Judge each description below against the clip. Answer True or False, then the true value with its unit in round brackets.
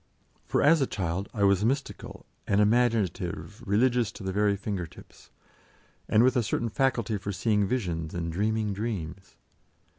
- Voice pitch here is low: True (105 Hz)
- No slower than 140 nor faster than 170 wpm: True (155 wpm)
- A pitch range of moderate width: True (3.5 semitones)